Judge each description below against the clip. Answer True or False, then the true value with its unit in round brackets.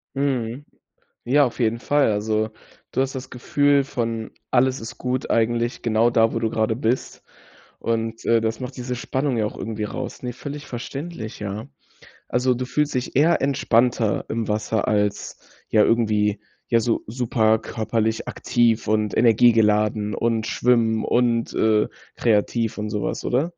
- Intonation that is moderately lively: False (2.3 semitones)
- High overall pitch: False (115 Hz)